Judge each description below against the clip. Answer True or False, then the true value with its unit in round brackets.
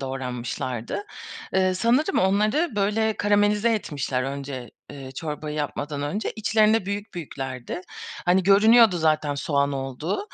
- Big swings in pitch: True (7.0 semitones)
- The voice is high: False (175 Hz)